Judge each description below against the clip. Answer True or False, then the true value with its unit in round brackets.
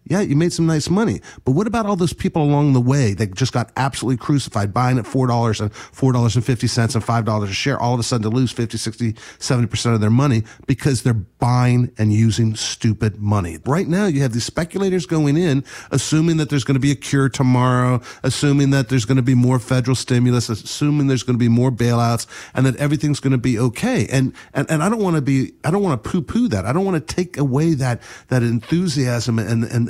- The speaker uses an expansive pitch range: False (3.6 semitones)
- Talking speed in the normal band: False (230 wpm)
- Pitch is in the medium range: False (130 Hz)